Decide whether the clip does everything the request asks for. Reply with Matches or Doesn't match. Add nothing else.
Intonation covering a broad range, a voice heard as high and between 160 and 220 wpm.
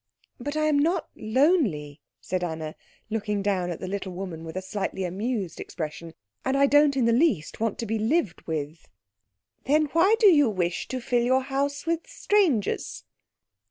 Matches